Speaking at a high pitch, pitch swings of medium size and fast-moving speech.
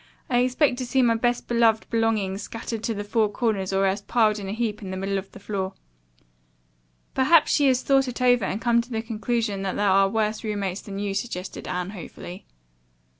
Yes: high, 215 Hz; average, 3.4 semitones; fast, 210 wpm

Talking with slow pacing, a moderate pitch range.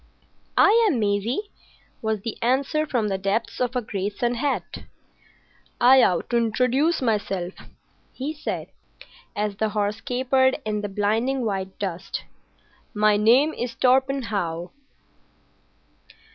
Yes: slow, 125 wpm; average, 4.3 semitones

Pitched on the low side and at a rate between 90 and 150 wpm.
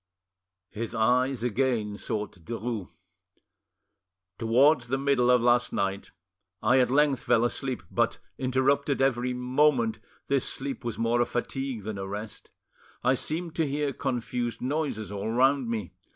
Yes: low, 125 Hz; average, 140 wpm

